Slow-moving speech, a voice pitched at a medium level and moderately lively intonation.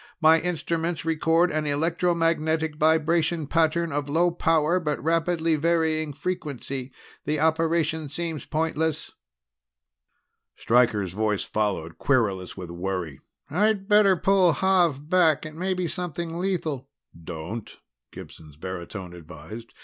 Yes: slow, 115 wpm; medium, 160 Hz; average, 5.0 semitones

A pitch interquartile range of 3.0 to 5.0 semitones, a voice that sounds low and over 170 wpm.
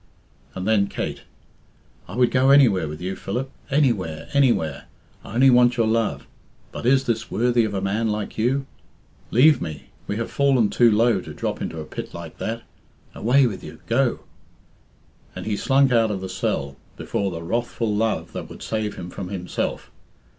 Yes: average, 4.3 semitones; low, 110 Hz; average, 180 wpm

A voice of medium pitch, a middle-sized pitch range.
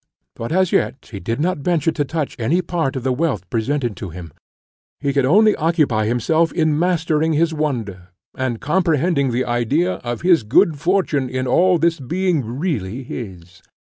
No: medium, 145 Hz; wide, 5.7 semitones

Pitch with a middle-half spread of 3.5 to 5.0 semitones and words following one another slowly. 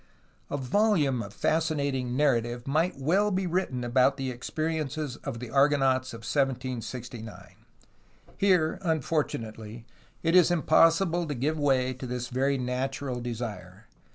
Yes: average, 4.3 semitones; slow, 130 wpm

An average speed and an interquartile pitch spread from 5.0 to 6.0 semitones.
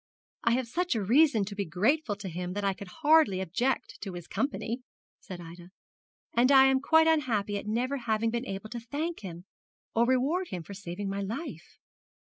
Yes: average, 195 wpm; wide, 5.5 semitones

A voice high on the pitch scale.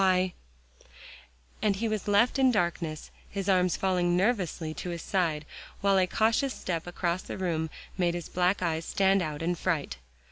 No: medium, 180 Hz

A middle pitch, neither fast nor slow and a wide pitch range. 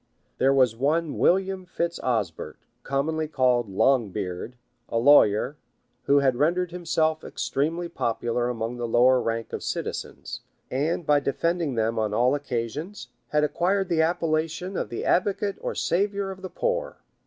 Yes: medium, 145 Hz; average, 150 wpm; wide, 6.1 semitones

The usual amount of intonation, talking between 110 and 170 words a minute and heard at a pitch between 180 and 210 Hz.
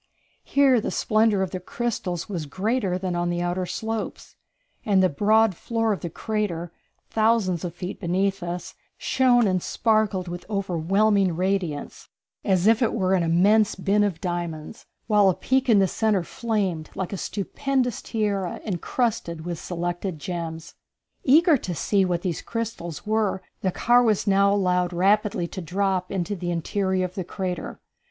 Yes: average, 3.5 semitones; average, 160 wpm; high, 190 Hz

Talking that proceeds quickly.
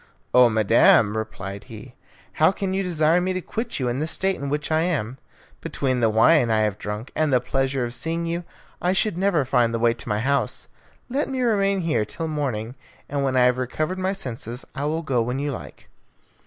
Yes: fast, 215 wpm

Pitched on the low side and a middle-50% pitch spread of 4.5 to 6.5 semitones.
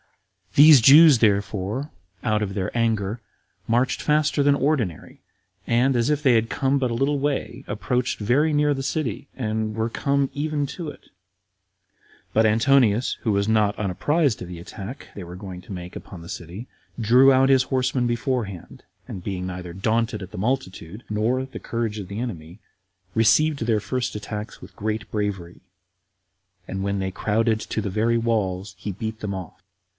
Yes: low, 115 Hz; average, 4.8 semitones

